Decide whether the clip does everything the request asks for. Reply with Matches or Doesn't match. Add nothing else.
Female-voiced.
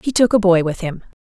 Matches